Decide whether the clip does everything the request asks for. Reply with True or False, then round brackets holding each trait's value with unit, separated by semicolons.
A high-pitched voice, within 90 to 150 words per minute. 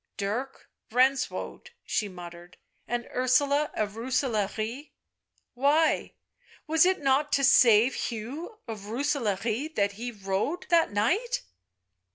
True (250 Hz; 140 wpm)